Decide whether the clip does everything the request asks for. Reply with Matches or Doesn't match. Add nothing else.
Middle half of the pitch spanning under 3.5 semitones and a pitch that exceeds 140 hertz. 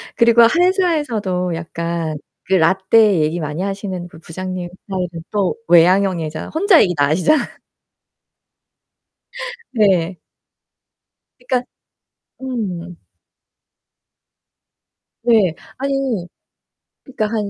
Doesn't match